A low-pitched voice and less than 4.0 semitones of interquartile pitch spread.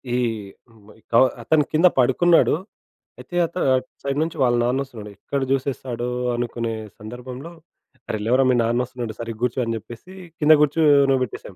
Yes: low, 125 Hz; average, 3.2 semitones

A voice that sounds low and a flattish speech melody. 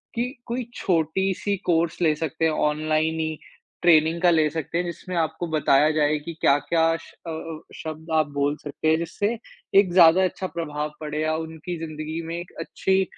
No: medium, 160 Hz; narrow, 1.9 semitones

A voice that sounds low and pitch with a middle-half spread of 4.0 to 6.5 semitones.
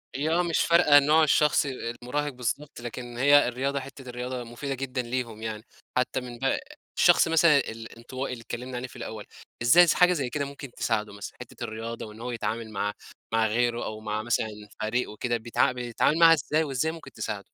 No: low, 125 Hz; average, 3.3 semitones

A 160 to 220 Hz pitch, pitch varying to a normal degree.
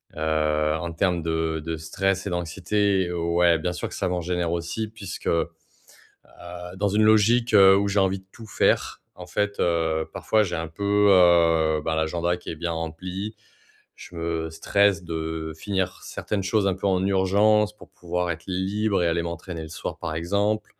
No: very low, 90 Hz; average, 3.3 semitones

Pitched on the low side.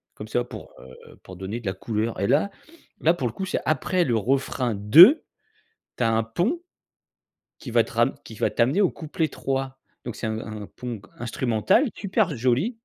Yes: low, 120 Hz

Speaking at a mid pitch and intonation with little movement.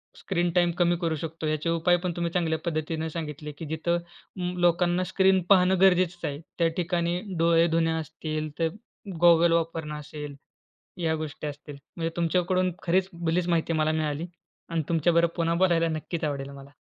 Yes: medium, 165 Hz; narrow, 1.8 semitones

